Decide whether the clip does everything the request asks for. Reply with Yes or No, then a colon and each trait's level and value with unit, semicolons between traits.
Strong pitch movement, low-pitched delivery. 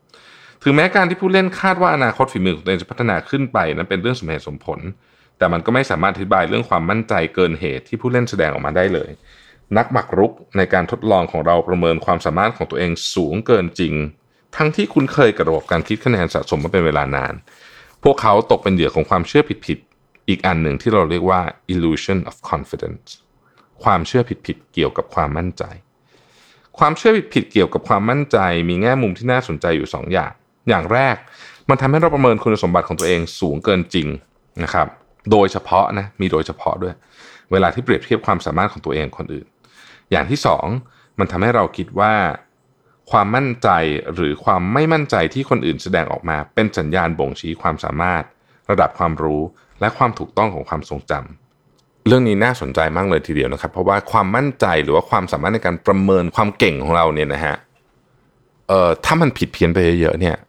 Yes: wide, 6.9 semitones; very low, 95 Hz